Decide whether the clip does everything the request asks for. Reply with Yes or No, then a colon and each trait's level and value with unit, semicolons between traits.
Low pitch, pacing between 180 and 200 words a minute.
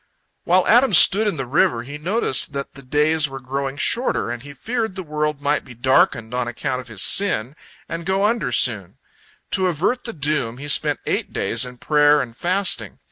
No: medium, 145 Hz; average, 195 wpm